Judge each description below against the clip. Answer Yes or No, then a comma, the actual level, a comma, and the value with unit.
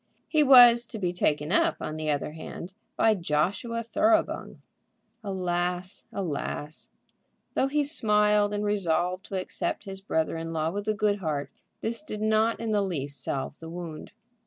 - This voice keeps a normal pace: Yes, average, 160 wpm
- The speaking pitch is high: Yes, high, 195 Hz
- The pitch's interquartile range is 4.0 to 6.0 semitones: Yes, average, 5.0 semitones